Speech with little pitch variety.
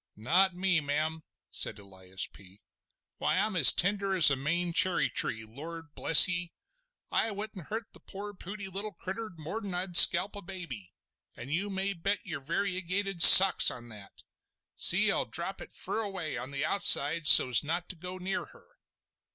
No: average, 4.9 semitones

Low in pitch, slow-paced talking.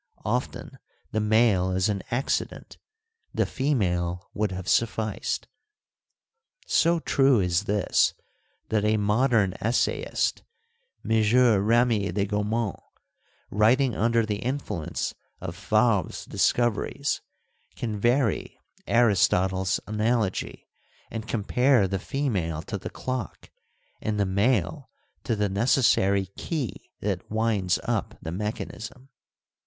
Yes: low, 105 Hz; slow, 110 wpm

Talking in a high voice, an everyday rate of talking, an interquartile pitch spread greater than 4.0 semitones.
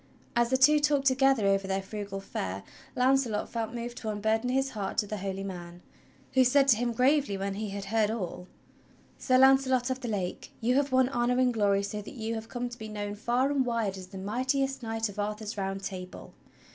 No: high, 225 Hz; fast, 215 wpm; average, 4.4 semitones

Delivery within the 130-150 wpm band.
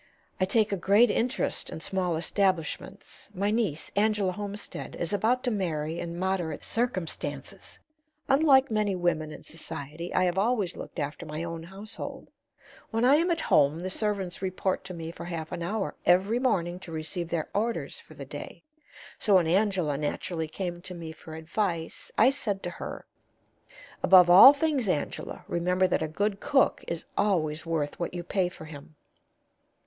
No: average, 170 wpm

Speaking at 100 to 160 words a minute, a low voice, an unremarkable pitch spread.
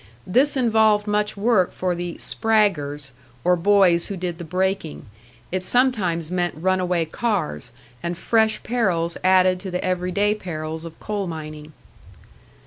No: average, 140 wpm; medium, 185 Hz; average, 3.6 semitones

